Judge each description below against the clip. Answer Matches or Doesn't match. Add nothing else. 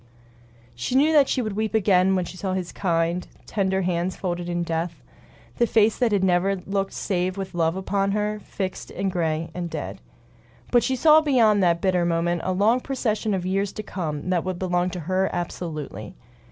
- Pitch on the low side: Doesn't match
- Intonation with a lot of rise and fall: Doesn't match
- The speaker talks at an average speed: Matches